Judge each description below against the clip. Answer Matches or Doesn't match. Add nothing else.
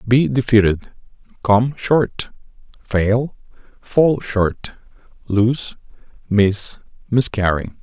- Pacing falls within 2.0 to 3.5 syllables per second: Matches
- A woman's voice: Doesn't match